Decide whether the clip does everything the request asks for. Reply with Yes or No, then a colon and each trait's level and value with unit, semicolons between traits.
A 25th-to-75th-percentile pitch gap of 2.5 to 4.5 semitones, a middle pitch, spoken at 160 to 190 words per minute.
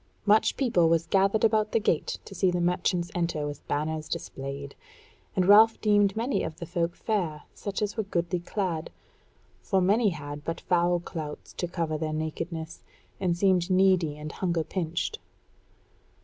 Yes: average, 3.8 semitones; medium, 175 Hz; average, 165 wpm